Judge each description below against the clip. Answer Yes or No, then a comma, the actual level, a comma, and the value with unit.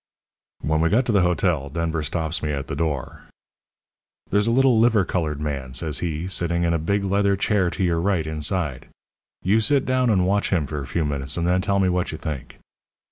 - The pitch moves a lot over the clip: No, average, 4.5 semitones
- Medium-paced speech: No, fast, 215 wpm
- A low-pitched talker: Yes, very low, 85 Hz